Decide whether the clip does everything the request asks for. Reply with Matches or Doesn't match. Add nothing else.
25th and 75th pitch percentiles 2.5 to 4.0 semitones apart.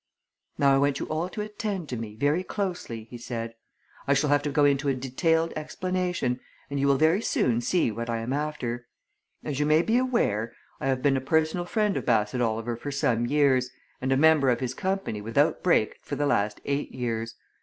Doesn't match